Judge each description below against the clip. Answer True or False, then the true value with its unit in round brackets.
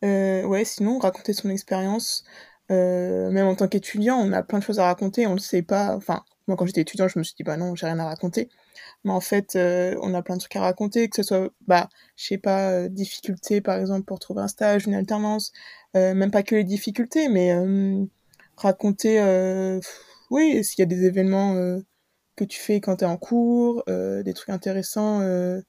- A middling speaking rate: False (225 wpm)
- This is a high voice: True (195 Hz)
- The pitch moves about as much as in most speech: False (2.2 semitones)